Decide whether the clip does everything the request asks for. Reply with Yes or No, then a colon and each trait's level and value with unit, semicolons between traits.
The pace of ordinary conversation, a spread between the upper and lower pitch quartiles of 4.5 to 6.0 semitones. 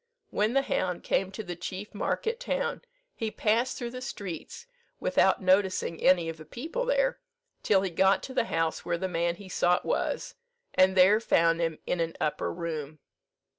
Yes: average, 180 wpm; wide, 5.4 semitones